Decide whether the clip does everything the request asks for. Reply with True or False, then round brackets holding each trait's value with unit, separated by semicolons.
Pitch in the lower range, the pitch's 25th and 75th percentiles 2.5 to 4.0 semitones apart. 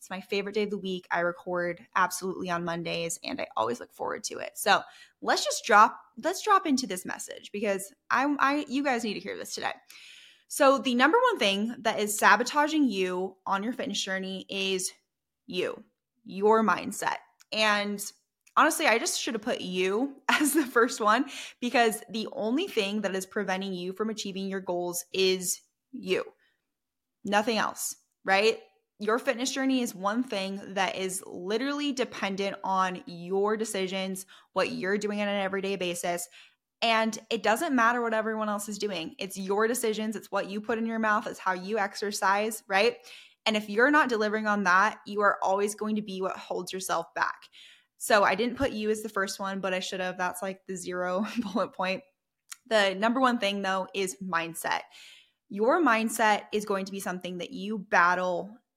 False (205 Hz; 3.4 semitones)